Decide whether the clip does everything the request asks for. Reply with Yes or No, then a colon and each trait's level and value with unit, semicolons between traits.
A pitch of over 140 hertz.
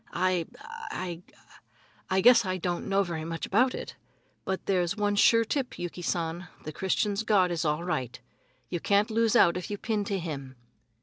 Yes: medium, 185 Hz